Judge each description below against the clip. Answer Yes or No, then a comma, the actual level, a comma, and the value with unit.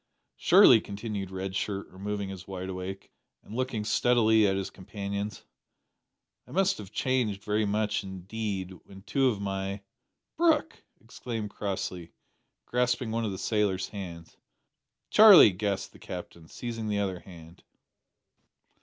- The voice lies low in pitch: Yes, low, 100 Hz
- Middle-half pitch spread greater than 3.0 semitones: No, average, 2.7 semitones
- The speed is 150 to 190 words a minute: No, slow, 135 wpm